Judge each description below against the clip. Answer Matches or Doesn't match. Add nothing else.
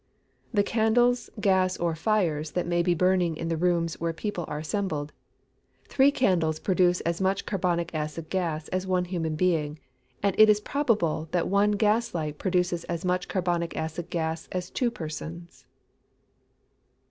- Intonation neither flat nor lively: Matches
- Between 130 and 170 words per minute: Matches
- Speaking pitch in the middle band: Matches